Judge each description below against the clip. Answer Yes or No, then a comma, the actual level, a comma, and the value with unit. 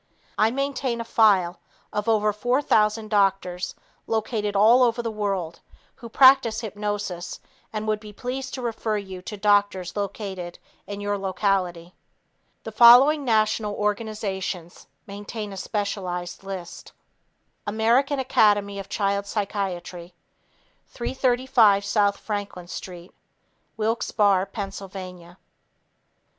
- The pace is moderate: No, slow, 110 wpm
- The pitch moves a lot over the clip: No, narrow, 2.4 semitones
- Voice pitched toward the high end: Yes, high, 205 Hz